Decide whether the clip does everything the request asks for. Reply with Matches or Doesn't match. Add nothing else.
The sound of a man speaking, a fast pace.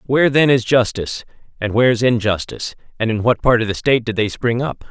Matches